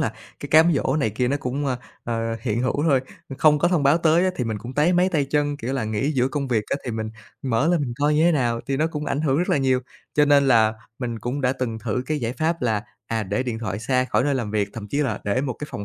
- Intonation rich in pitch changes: No, average, 4.3 semitones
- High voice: No, low, 130 Hz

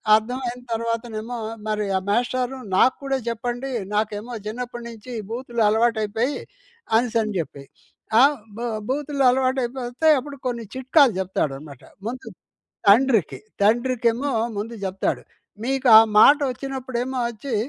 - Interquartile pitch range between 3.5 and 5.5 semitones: No, average, 2.9 semitones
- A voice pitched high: Yes, high, 240 Hz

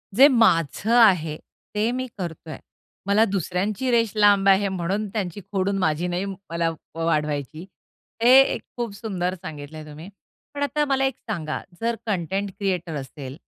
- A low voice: No, high, 190 Hz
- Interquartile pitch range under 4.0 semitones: No, average, 4.7 semitones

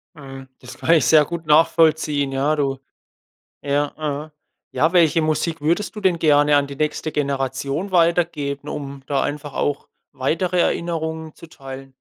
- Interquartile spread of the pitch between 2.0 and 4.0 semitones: Yes, narrow, 2.5 semitones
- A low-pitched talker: No, medium, 150 Hz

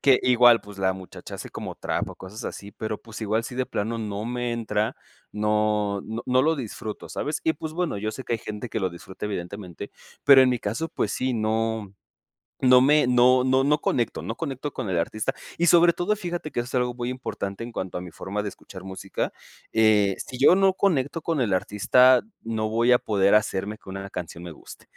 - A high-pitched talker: No, low, 115 Hz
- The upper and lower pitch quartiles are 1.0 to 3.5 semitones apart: No, average, 4.0 semitones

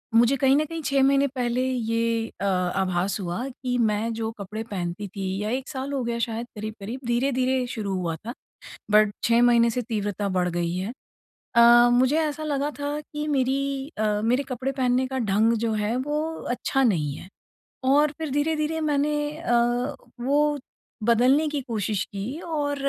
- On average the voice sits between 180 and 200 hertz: No, high, 245 Hz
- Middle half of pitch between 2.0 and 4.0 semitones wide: No, average, 4.4 semitones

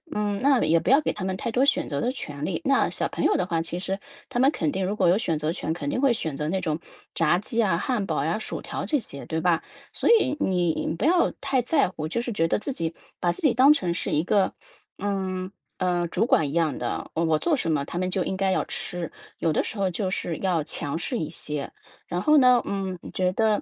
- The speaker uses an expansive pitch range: Yes, wide, 5.8 semitones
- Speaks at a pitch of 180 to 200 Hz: Yes, medium, 185 Hz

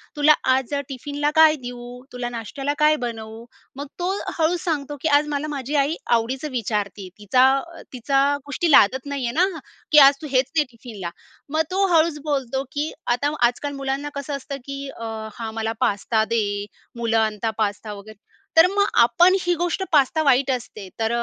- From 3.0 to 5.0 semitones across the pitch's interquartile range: Yes, average, 4.3 semitones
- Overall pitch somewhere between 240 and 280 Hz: Yes, very high, 270 Hz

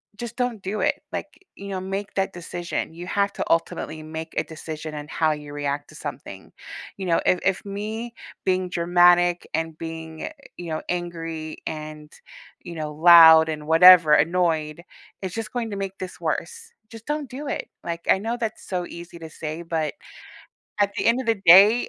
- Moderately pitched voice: Yes, medium, 175 Hz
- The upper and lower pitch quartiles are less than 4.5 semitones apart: Yes, average, 3.8 semitones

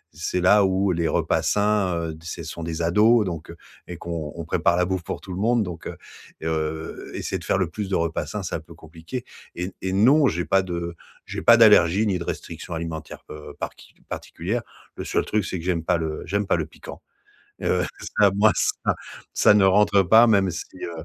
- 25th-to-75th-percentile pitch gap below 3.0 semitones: No, average, 3.5 semitones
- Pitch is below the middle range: Yes, very low, 90 Hz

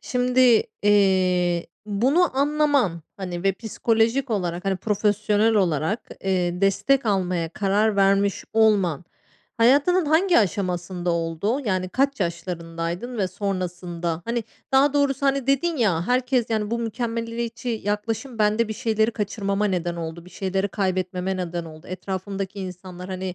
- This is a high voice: Yes, high, 200 Hz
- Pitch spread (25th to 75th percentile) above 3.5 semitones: Yes, average, 4.3 semitones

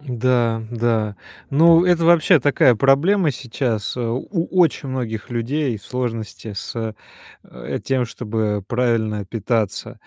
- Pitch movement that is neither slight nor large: Yes, average, 3.9 semitones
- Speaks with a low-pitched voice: Yes, low, 120 Hz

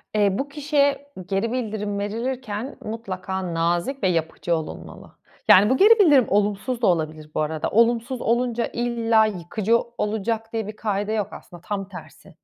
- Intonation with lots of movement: No, average, 3.9 semitones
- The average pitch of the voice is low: No, high, 215 Hz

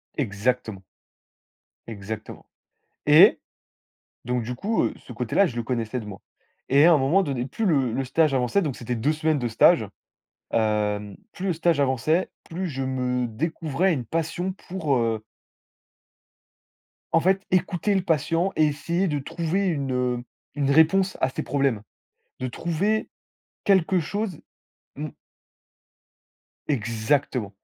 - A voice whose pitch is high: No, medium, 140 Hz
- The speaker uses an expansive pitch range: Yes, wide, 5.7 semitones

